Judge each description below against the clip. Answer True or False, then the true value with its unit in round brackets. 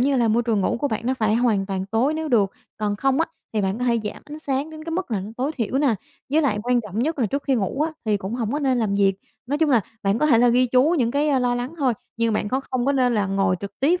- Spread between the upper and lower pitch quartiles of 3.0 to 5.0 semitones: True (4.7 semitones)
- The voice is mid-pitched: False (245 Hz)